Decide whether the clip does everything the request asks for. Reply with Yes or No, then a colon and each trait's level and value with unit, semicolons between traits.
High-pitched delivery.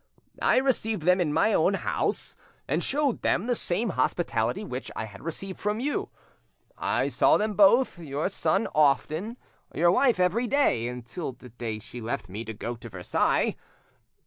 No: medium, 170 Hz